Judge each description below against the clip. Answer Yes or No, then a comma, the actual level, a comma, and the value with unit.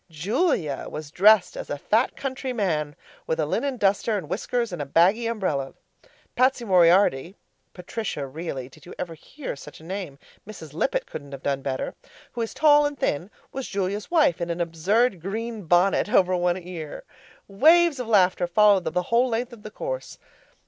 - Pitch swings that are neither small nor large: No, wide, 6.2 semitones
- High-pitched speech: Yes, high, 195 Hz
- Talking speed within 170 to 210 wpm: Yes, average, 175 wpm